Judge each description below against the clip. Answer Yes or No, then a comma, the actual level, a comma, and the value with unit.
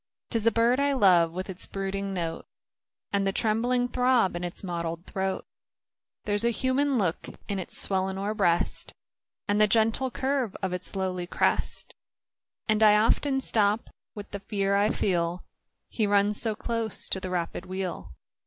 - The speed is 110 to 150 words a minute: No, average, 165 wpm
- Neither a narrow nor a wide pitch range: Yes, average, 3.4 semitones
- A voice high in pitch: Yes, high, 200 Hz